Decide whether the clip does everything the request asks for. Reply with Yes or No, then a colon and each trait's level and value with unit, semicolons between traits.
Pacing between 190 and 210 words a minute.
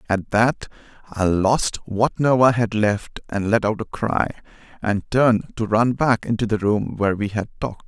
Yes: average, 200 wpm